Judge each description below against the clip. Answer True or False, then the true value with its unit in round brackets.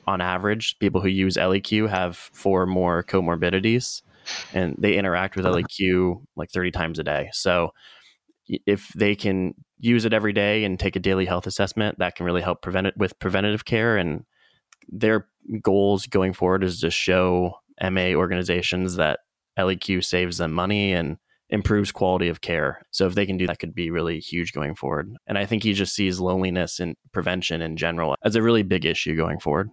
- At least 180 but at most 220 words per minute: True (190 wpm)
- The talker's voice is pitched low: True (95 Hz)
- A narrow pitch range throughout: True (2.3 semitones)